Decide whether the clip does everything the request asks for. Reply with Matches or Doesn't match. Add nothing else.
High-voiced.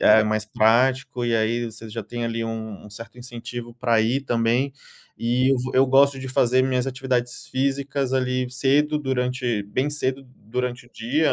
Doesn't match